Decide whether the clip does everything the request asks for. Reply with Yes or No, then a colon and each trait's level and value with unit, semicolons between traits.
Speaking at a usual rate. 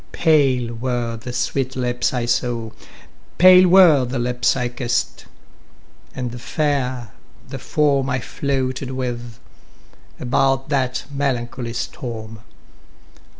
No: slow, 110 wpm